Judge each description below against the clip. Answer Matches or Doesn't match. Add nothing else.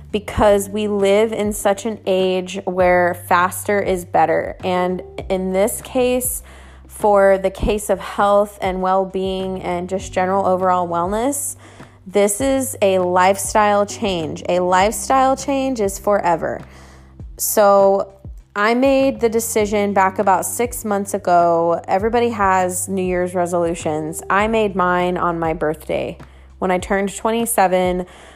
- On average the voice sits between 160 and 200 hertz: Matches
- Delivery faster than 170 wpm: Doesn't match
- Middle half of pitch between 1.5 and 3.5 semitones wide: Matches